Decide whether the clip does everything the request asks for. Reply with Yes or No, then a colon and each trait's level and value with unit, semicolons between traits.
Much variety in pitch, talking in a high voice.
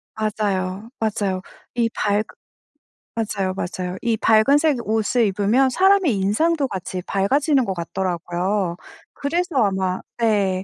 No: average, 4.8 semitones; high, 210 Hz